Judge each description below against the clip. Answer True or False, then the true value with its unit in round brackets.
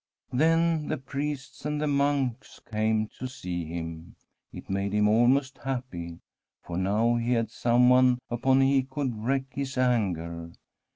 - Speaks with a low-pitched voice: True (125 Hz)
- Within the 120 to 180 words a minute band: True (150 wpm)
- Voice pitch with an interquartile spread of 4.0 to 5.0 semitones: True (4.5 semitones)